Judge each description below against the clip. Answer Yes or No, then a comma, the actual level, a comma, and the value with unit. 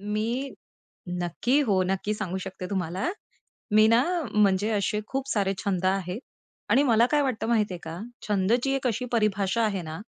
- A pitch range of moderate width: Yes, average, 3.6 semitones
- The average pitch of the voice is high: Yes, high, 210 Hz